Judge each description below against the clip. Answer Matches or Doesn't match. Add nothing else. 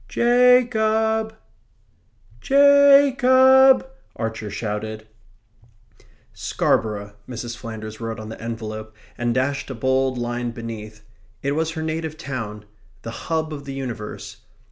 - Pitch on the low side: Matches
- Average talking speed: Doesn't match